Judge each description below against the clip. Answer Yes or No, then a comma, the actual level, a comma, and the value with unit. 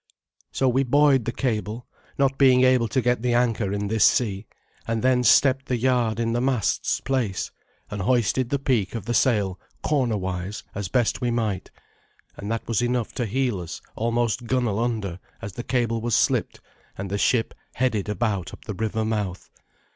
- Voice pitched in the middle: No, low, 115 Hz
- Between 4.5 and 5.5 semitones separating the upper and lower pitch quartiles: No, average, 3.2 semitones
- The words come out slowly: No, average, 185 wpm